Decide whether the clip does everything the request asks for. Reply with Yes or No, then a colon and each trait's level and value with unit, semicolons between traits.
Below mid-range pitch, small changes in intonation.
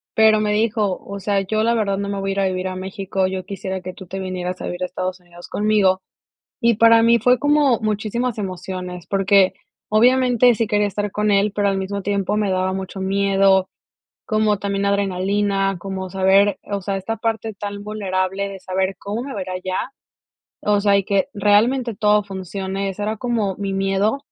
No: high, 200 Hz; narrow, 2.0 semitones